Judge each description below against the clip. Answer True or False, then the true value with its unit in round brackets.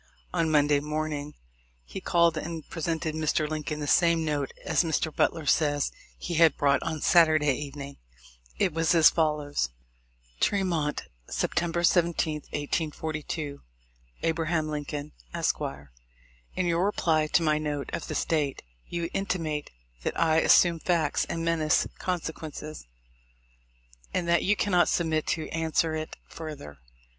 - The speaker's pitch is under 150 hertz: False (155 Hz)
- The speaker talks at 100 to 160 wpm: True (140 wpm)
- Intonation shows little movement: True (2.1 semitones)